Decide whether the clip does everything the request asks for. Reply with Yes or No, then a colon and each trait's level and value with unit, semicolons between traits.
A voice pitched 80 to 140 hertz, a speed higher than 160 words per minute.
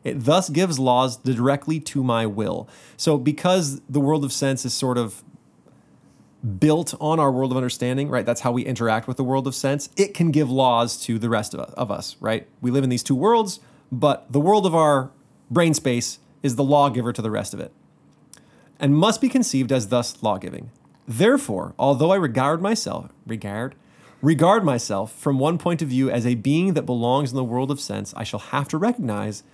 Yes: low, 135 Hz; average, 200 wpm